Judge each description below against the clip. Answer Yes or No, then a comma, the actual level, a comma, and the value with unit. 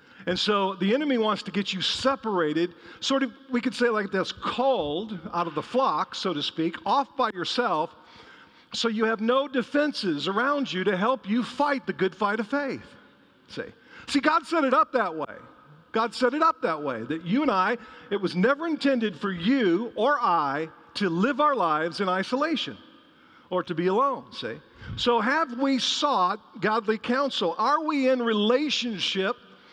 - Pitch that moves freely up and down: Yes, wide, 5.8 semitones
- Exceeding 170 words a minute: Yes, average, 180 wpm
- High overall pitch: Yes, high, 235 Hz